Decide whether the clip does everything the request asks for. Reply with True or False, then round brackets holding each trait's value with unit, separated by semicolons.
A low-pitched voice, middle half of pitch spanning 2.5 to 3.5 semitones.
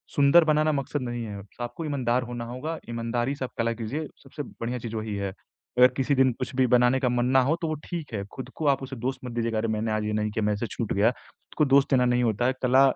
True (125 Hz; 2.8 semitones)